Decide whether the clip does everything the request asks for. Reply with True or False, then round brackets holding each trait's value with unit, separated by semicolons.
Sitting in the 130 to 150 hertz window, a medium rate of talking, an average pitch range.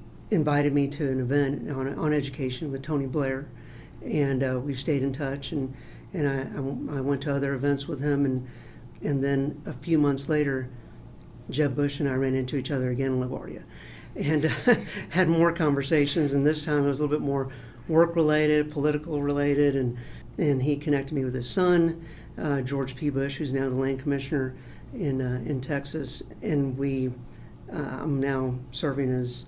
False (140 Hz; 190 wpm; 1.9 semitones)